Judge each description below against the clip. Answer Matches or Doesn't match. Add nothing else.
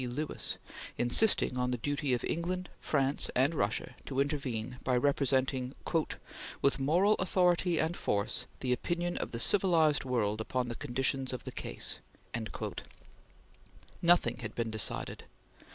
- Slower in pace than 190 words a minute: Matches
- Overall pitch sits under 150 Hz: Matches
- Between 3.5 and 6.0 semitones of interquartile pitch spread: Matches